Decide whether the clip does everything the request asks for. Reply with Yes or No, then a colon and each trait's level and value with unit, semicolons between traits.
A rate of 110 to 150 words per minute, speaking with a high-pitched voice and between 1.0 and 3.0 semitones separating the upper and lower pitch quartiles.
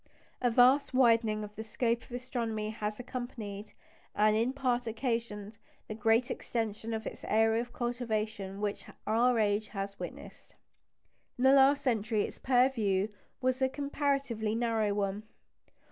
Yes: average, 145 wpm; high, 225 Hz; average, 2.7 semitones